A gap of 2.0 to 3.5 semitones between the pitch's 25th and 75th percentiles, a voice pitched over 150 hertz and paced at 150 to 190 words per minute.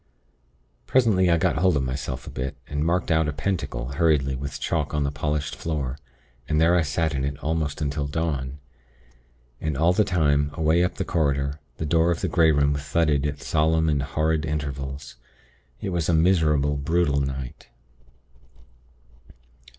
No: narrow, 2.5 semitones; very low, 75 Hz; average, 165 wpm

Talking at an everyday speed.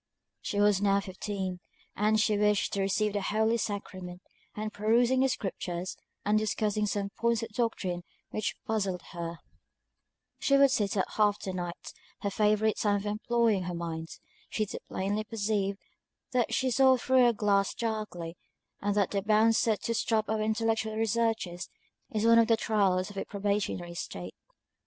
Yes: average, 165 wpm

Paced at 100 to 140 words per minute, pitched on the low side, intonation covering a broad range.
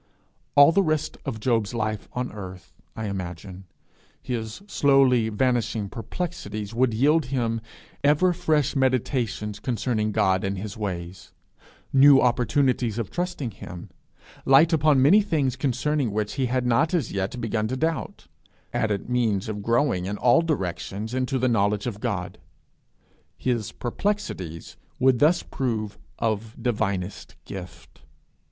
No: slow, 135 wpm; low, 120 Hz; average, 4.7 semitones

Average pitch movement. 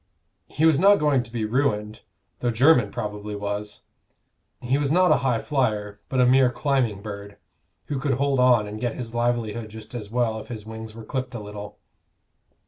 Yes: average, 3.8 semitones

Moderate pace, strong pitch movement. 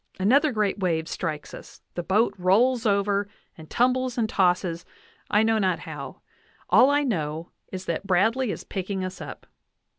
No: average, 160 wpm; average, 4.2 semitones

